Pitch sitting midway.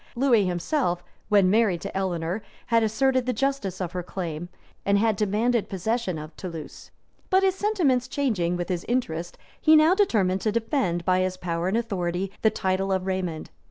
No: high, 195 Hz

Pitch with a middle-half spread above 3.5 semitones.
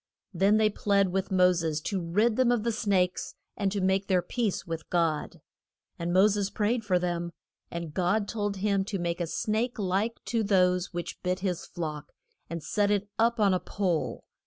No: average, 3.0 semitones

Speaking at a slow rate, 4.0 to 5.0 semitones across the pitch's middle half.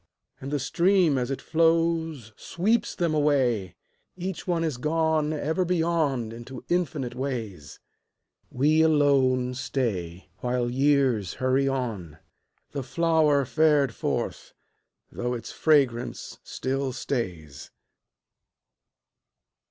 Yes: slow, 105 wpm; average, 4.5 semitones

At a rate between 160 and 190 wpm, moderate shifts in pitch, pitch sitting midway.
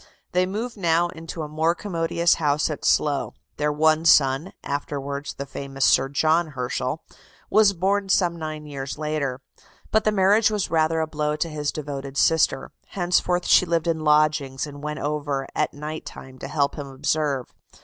Yes: average, 170 wpm; average, 3.0 semitones; medium, 155 Hz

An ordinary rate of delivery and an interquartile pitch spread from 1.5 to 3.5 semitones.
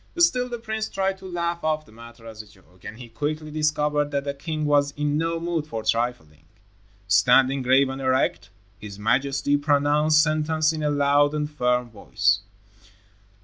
No: average, 175 wpm; average, 4.1 semitones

